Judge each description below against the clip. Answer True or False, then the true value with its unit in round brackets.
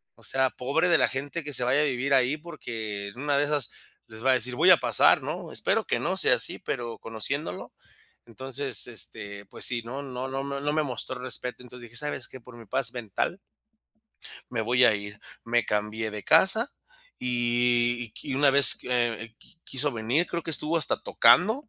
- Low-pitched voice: True (125 Hz)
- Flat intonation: False (3.5 semitones)